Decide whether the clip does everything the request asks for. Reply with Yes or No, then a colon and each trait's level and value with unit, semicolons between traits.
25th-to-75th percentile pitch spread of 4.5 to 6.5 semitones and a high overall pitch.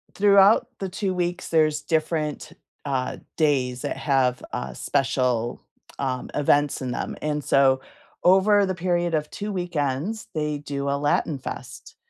No: average, 4.8 semitones; medium, 150 Hz